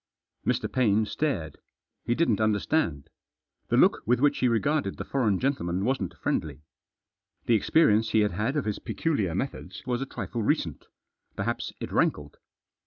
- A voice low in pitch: Yes, low, 110 Hz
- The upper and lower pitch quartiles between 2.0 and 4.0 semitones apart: No, average, 5.2 semitones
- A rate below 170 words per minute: Yes, average, 155 wpm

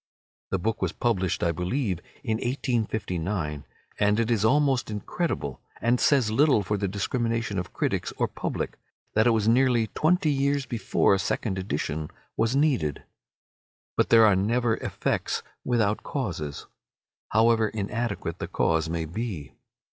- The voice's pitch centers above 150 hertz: No, low, 110 Hz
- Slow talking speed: No, average, 145 wpm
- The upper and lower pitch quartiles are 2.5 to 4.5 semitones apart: Yes, average, 4.2 semitones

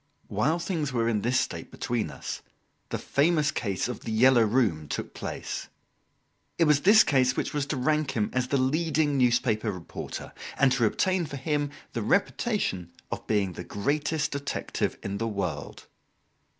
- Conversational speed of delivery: Yes, average, 165 wpm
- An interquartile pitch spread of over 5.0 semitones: Yes, wide, 5.5 semitones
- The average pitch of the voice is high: No, low, 130 Hz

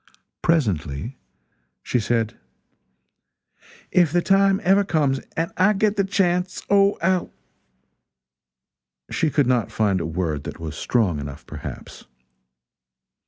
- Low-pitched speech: Yes, low, 130 Hz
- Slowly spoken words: Yes, slow, 120 wpm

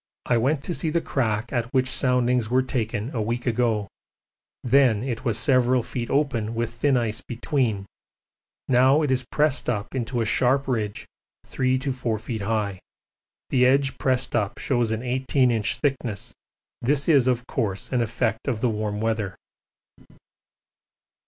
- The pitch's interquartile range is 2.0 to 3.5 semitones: Yes, average, 2.8 semitones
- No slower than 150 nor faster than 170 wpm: Yes, average, 160 wpm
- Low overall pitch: Yes, low, 120 Hz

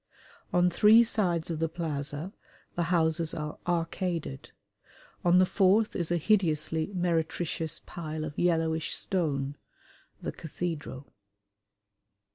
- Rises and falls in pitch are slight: Yes, narrow, 2.2 semitones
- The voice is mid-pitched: Yes, medium, 165 Hz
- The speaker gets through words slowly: Yes, slow, 110 wpm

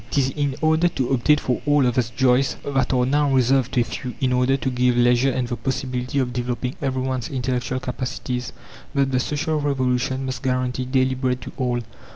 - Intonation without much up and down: Yes, narrow, 1.4 semitones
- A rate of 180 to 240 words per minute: Yes, average, 200 wpm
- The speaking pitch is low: Yes, low, 130 Hz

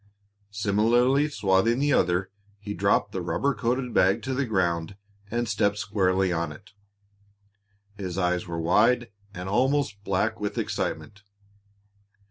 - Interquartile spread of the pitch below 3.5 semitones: No, average, 4.3 semitones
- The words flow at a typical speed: No, slow, 130 wpm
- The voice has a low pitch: Yes, low, 105 Hz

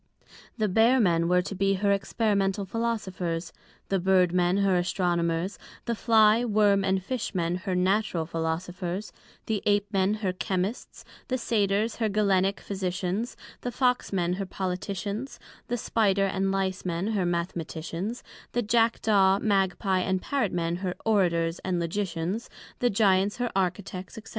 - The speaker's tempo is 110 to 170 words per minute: Yes, average, 150 wpm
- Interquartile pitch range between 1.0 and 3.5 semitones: Yes, average, 2.9 semitones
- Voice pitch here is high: Yes, high, 195 Hz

